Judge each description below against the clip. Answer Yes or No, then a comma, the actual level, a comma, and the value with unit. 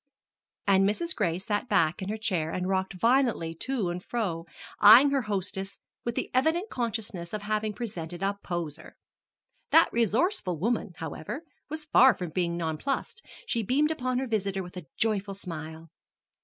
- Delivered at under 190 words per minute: Yes, average, 160 wpm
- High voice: Yes, high, 200 Hz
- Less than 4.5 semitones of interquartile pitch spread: No, average, 5.3 semitones